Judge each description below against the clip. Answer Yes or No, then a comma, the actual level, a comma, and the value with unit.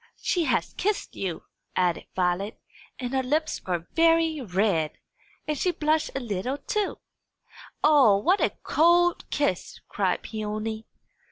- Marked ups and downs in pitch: Yes, wide, 8.2 semitones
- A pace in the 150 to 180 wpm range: No, slow, 135 wpm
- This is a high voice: Yes, very high, 255 Hz